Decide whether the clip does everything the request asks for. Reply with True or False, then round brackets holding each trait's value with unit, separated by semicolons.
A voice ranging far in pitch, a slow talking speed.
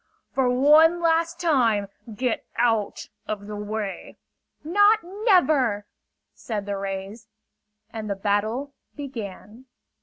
True (7.1 semitones; 110 wpm)